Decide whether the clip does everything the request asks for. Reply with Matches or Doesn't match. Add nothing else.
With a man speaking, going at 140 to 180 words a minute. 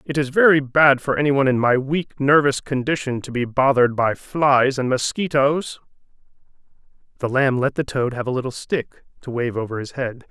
Doesn't match